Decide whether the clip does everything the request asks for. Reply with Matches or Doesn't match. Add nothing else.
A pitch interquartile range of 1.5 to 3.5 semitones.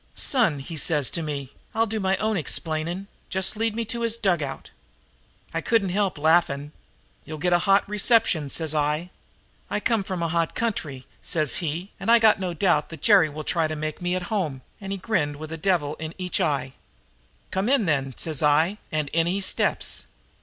Doesn't match